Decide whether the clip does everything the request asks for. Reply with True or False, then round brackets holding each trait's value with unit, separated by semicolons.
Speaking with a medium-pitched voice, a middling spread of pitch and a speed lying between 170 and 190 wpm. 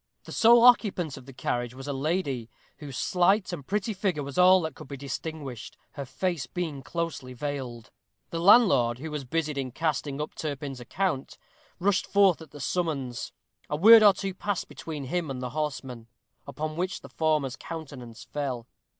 True (150 Hz; 5.0 semitones; 175 wpm)